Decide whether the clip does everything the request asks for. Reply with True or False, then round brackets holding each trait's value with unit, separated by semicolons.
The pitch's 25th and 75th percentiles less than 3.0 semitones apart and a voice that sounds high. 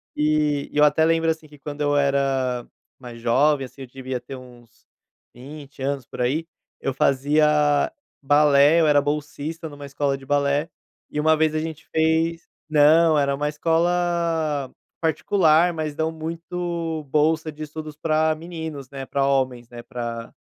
False (2.5 semitones; 150 Hz)